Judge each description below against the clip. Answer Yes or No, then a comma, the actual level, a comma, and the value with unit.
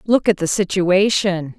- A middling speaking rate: Yes, average, 150 wpm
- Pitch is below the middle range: No, high, 190 Hz